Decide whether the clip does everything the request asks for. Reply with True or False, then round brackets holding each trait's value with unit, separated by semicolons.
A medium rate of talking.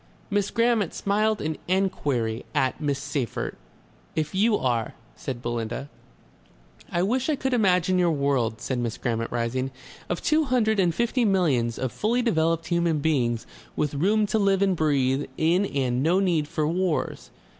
True (160 wpm)